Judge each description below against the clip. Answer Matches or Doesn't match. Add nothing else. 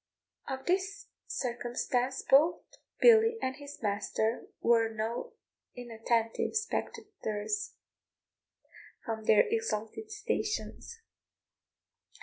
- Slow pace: Matches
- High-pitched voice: Matches